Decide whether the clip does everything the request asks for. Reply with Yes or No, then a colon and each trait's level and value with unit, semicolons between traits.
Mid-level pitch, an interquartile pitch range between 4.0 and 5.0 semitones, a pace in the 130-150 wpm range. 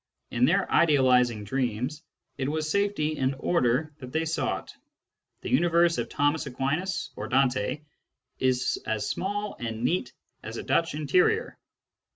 Yes: medium, 145 Hz; average, 4.6 semitones; average, 140 wpm